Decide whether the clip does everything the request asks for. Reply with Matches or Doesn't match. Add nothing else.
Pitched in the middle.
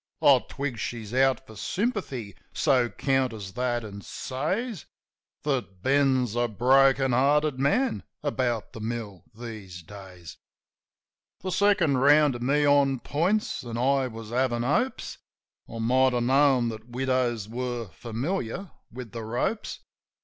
Doesn't match